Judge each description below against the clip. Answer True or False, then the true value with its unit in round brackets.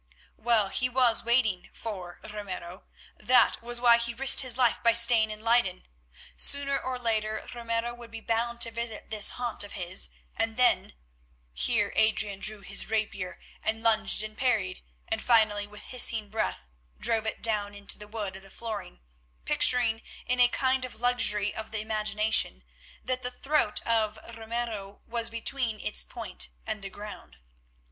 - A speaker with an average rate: True (160 wpm)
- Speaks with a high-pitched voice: True (220 Hz)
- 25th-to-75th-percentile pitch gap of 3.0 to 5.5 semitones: False (2.5 semitones)